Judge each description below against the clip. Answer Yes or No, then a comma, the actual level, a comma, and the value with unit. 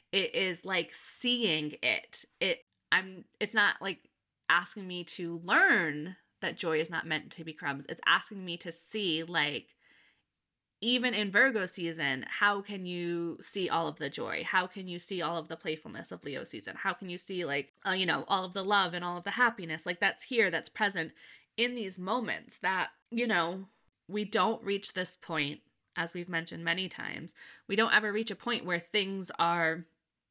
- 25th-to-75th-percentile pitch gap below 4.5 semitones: Yes, average, 3.8 semitones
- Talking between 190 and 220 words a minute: Yes, average, 195 wpm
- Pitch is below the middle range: No, medium, 185 Hz